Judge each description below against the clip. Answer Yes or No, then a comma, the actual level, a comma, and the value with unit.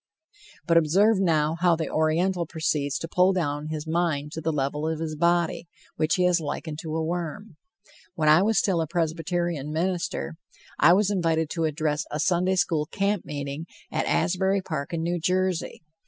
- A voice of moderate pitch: Yes, medium, 165 Hz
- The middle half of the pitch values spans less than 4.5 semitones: Yes, narrow, 2.6 semitones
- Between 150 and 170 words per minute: No, average, 180 wpm